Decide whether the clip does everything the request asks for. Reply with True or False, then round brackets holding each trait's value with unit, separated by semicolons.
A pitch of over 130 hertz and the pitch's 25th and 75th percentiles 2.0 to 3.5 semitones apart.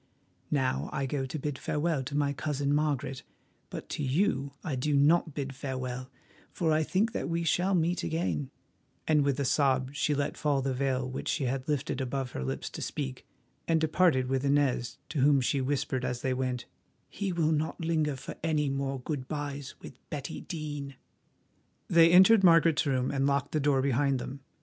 True (140 Hz; 2.8 semitones)